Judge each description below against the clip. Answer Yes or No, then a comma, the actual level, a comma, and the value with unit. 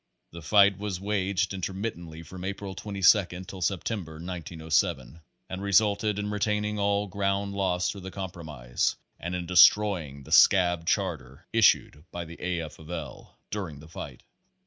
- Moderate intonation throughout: Yes, average, 3.3 semitones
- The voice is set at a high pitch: No, very low, 95 Hz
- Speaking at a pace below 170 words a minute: Yes, average, 155 wpm